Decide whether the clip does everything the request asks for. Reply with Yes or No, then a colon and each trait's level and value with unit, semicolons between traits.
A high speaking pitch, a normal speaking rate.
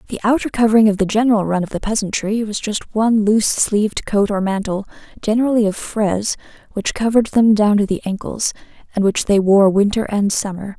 Yes: high, 210 Hz; average, 195 wpm